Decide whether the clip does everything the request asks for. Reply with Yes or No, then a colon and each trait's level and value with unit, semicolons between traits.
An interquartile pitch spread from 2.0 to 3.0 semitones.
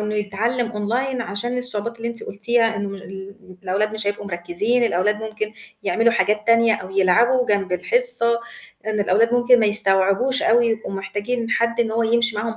Yes: narrow, 2.6 semitones